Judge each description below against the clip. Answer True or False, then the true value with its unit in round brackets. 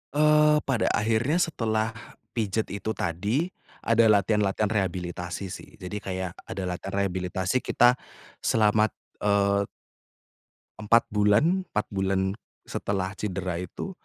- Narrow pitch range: False (3.1 semitones)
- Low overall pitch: True (105 Hz)